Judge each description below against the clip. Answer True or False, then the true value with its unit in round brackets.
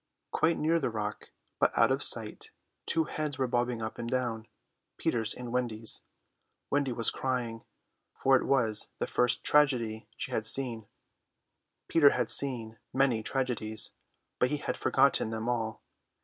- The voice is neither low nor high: False (120 Hz)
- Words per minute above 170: False (150 wpm)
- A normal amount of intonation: True (3.2 semitones)